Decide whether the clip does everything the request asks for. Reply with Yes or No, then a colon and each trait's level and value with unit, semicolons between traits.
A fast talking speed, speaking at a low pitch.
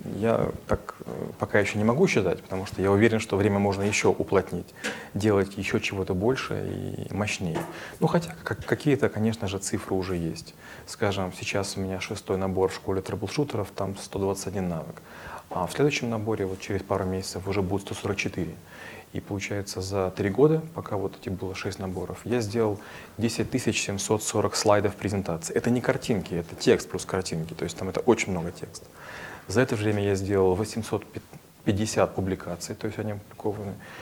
Yes: fast, 170 wpm; low, 100 Hz